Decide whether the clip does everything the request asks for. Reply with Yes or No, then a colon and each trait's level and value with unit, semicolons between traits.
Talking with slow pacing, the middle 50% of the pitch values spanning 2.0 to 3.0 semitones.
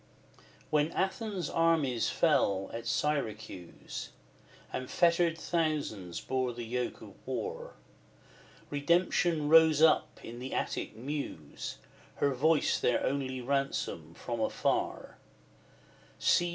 No: slow, 110 wpm; wide, 5.4 semitones